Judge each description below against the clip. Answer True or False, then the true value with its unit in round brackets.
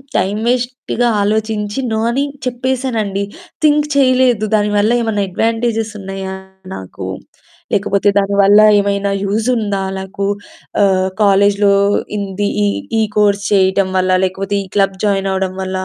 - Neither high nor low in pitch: False (205 Hz)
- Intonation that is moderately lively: False (2.3 semitones)